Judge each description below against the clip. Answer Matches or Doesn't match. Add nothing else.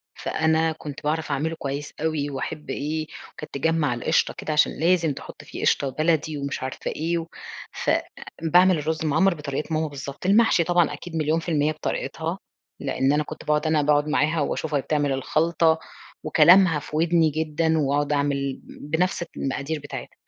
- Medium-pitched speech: Matches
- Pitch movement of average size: Doesn't match